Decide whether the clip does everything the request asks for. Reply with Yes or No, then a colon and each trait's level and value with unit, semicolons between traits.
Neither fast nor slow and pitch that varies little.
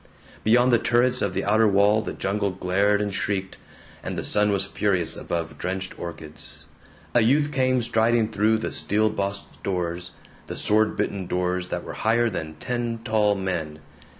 No: average, 170 wpm; average, 3.3 semitones